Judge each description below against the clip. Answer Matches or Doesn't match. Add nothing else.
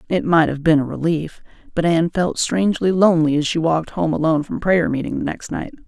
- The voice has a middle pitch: Matches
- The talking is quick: Matches